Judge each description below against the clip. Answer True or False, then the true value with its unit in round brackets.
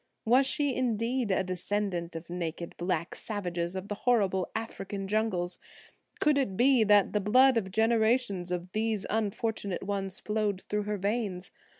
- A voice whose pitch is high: True (205 Hz)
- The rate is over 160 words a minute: False (155 wpm)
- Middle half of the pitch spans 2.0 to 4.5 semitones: True (3.4 semitones)